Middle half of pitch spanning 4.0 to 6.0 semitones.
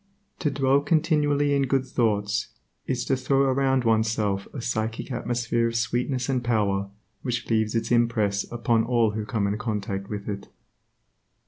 No: average, 3.5 semitones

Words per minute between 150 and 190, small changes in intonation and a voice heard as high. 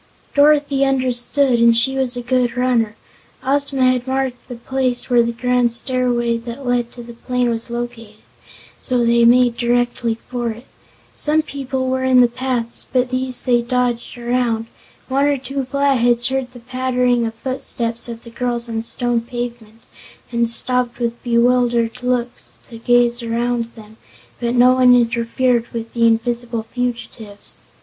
Yes: average, 160 wpm; narrow, 1.4 semitones; high, 245 Hz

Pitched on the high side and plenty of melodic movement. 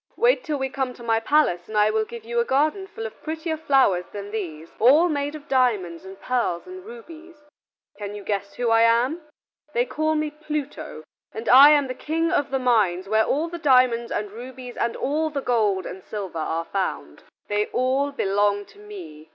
Yes: high, 245 Hz; wide, 6.3 semitones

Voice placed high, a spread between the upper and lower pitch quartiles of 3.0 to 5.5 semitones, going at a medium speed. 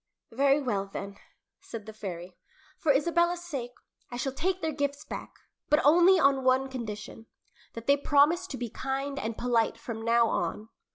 Yes: very high, 265 Hz; average, 4.3 semitones; average, 170 wpm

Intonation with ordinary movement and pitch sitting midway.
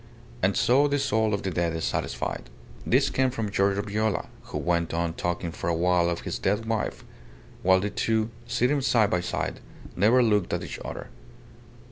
No: average, 4.4 semitones; low, 100 Hz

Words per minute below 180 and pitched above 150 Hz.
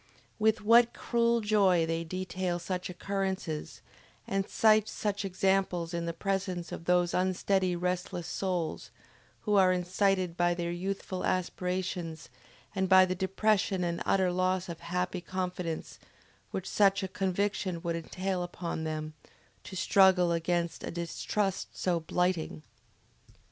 Yes: slow, 135 wpm; medium, 185 Hz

